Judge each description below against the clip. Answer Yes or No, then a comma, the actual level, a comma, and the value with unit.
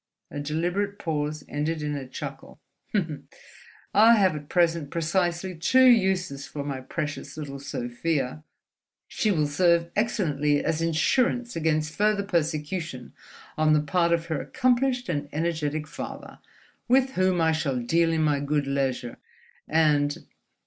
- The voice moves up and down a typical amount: Yes, average, 4.2 semitones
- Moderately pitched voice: Yes, medium, 160 Hz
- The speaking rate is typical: No, slow, 130 wpm